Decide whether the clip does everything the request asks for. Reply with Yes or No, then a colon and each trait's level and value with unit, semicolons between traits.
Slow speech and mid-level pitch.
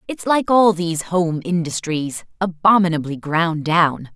Yes: slow, 130 wpm; medium, 175 Hz